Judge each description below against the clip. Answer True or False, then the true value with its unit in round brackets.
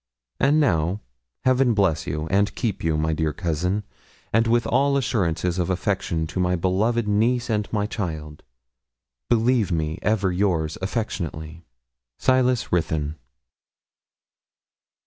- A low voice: True (95 Hz)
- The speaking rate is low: True (120 wpm)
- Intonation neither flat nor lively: False (5.9 semitones)